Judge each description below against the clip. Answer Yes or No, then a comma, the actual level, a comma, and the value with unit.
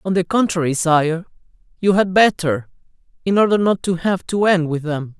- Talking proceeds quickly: No, average, 185 wpm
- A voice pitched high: No, medium, 175 Hz